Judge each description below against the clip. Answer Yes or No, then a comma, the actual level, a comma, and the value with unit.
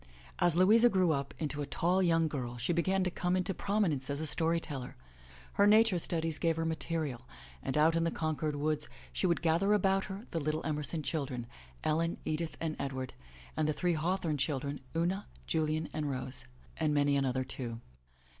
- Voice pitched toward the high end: No, medium, 160 Hz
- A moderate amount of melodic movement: Yes, average, 3.3 semitones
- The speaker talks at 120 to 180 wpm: No, average, 190 wpm